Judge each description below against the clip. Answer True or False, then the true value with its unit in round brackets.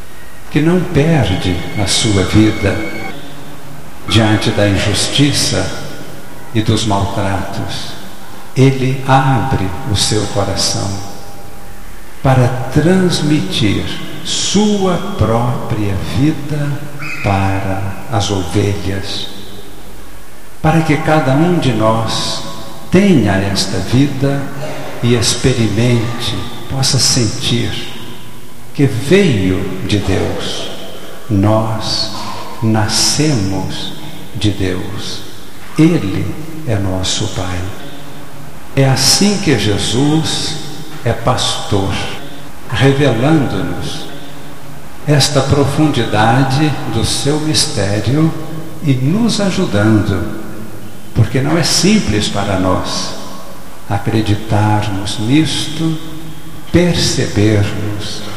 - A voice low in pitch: True (115 Hz)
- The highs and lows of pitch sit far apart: True (6.3 semitones)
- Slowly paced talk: True (75 wpm)